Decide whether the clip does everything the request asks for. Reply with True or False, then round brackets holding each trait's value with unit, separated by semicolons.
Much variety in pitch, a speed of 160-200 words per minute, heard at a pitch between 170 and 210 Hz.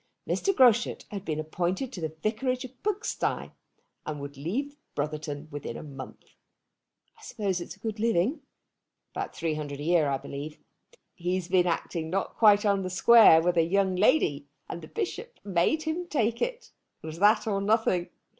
True (6.7 semitones; 175 wpm; 185 Hz)